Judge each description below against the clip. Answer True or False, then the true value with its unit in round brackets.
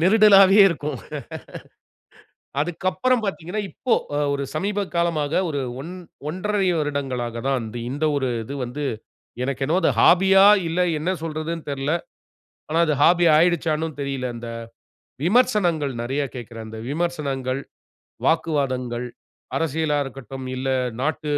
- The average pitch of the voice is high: False (155 Hz)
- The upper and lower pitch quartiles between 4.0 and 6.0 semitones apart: True (4.3 semitones)